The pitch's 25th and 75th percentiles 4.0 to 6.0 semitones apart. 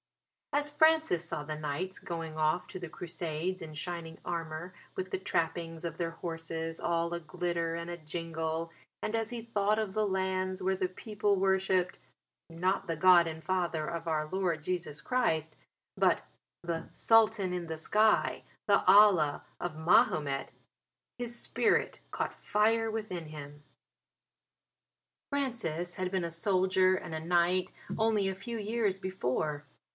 No: average, 3.0 semitones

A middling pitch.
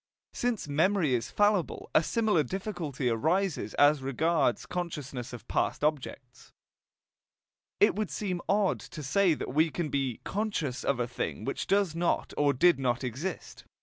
Yes: medium, 155 Hz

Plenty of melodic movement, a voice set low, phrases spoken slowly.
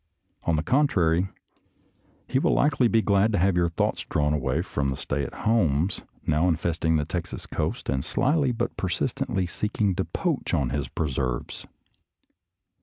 No: wide, 6.3 semitones; very low, 85 Hz; average, 160 wpm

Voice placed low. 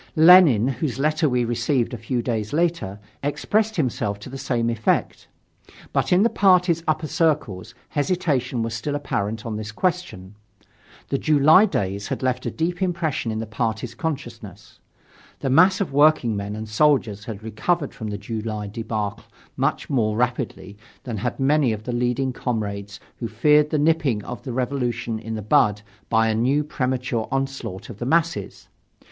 Yes: low, 125 Hz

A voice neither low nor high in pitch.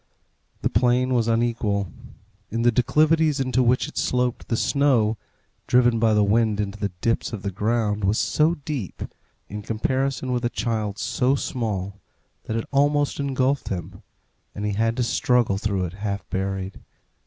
No: low, 115 Hz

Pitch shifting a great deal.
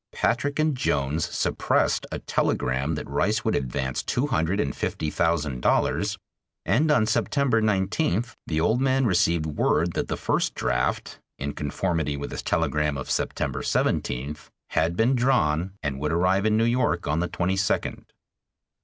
Yes: wide, 7.2 semitones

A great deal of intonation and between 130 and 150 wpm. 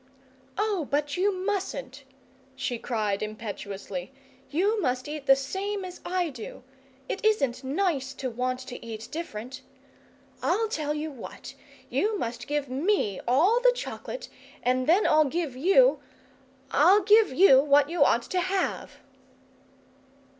Yes: wide, 7.0 semitones; average, 140 wpm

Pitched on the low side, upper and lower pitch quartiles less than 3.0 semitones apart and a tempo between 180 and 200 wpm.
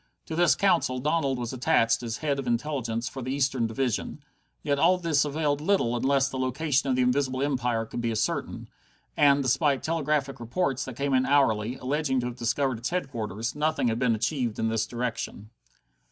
No: low, 130 Hz; average, 3.3 semitones; average, 185 wpm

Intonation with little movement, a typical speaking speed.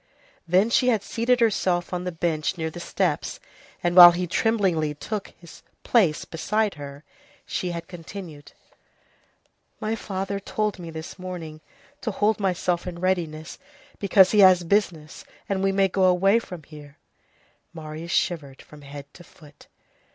No: average, 3.6 semitones; average, 150 wpm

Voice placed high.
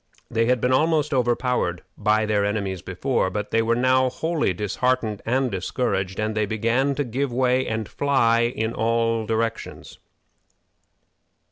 No: low, 115 Hz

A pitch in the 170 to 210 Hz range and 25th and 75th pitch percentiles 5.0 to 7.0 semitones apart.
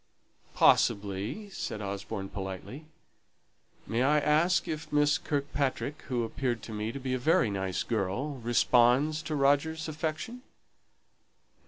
No: low, 130 Hz; wide, 5.5 semitones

